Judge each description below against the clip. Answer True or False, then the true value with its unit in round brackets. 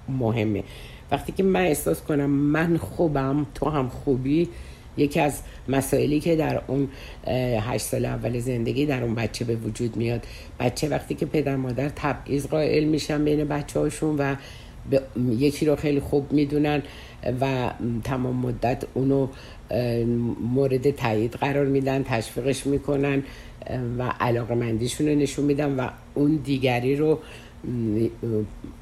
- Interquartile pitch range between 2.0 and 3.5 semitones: True (3.1 semitones)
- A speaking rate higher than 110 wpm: True (135 wpm)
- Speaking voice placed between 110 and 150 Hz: True (135 Hz)